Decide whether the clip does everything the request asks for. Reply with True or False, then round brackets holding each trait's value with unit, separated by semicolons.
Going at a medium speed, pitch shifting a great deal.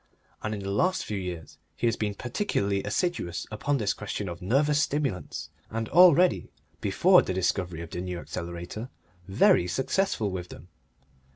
True (160 wpm; 7.5 semitones)